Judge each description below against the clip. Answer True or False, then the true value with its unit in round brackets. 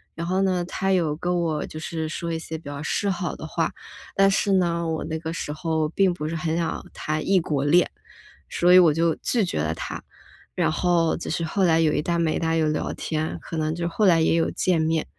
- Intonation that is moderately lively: False (2.0 semitones)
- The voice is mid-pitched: True (165 Hz)